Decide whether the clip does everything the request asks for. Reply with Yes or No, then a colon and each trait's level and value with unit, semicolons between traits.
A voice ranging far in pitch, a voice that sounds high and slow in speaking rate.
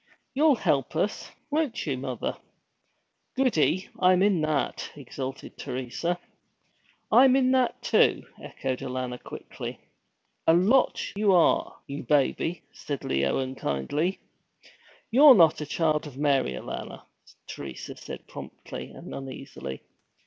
No: wide, 7.0 semitones; medium, 150 Hz; slow, 120 wpm